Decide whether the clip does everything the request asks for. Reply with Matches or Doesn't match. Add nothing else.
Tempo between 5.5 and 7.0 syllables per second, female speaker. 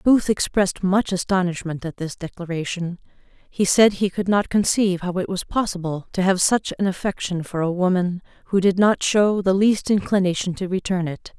Doesn't match